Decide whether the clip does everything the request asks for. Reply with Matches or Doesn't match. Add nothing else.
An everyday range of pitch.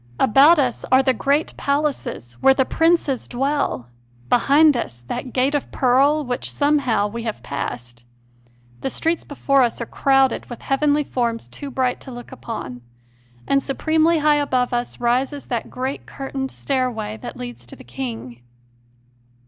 Matches